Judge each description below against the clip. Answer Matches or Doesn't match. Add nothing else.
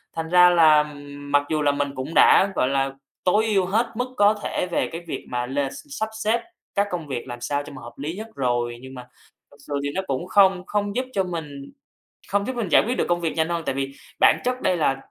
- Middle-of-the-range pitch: Matches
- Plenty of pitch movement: Matches